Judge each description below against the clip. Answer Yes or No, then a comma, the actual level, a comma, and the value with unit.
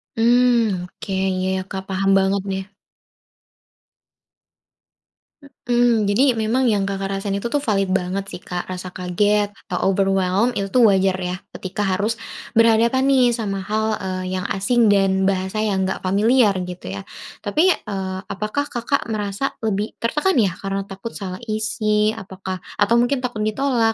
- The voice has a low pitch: No, high, 200 Hz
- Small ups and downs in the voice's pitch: No, average, 3.3 semitones